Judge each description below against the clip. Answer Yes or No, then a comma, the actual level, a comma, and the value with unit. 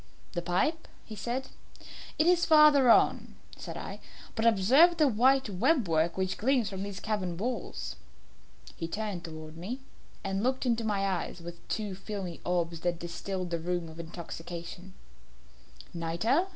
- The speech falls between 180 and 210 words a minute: No, average, 150 wpm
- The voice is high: Yes, high, 195 Hz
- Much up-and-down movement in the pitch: Yes, wide, 6.1 semitones